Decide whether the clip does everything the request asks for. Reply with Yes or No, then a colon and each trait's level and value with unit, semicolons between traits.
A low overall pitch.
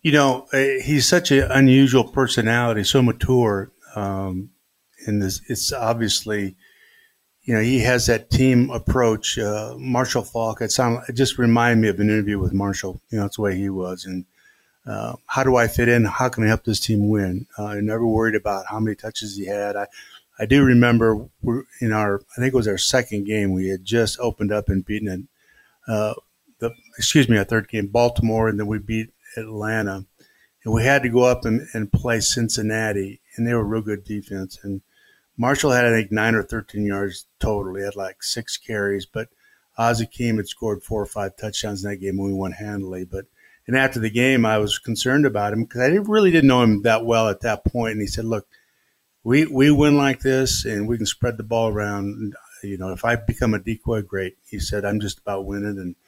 Yes: low, 110 Hz